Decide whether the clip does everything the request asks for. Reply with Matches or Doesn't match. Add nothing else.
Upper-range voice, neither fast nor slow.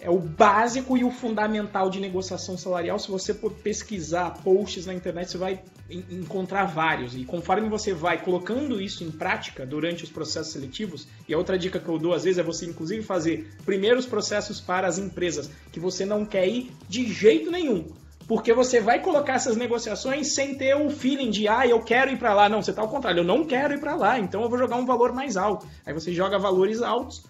Doesn't match